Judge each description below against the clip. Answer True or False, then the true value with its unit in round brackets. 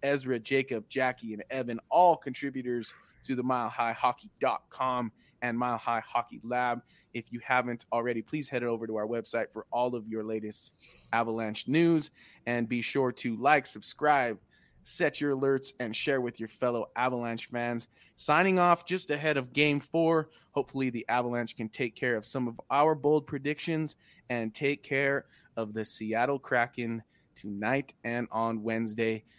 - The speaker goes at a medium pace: True (160 wpm)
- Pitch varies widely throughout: False (3.2 semitones)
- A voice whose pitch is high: False (125 Hz)